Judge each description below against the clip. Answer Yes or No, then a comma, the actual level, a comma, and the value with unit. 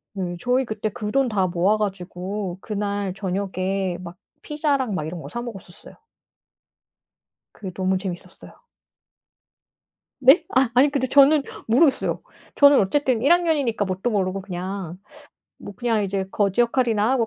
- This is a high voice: Yes, high, 205 Hz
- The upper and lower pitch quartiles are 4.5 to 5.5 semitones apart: Yes, average, 5.1 semitones